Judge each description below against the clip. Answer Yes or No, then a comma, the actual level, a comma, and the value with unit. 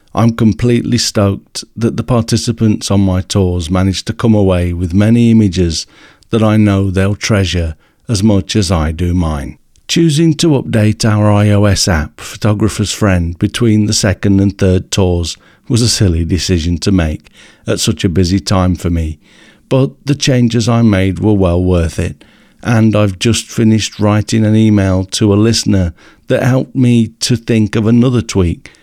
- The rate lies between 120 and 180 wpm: Yes, average, 170 wpm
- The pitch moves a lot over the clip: No, average, 3.5 semitones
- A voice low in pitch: Yes, low, 105 Hz